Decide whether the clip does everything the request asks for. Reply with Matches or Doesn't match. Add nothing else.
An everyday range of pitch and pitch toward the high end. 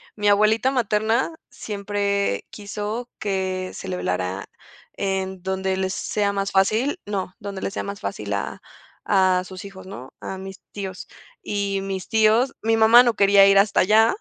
Doesn't match